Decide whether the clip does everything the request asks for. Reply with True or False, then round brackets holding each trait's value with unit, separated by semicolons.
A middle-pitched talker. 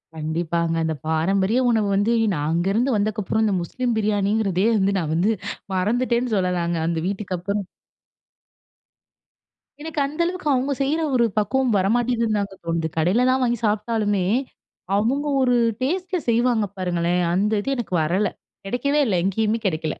False (210 Hz)